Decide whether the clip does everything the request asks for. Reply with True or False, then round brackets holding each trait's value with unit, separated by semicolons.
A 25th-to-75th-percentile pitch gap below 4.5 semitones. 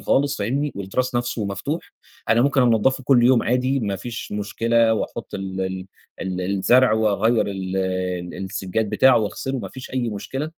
False (4.8 semitones)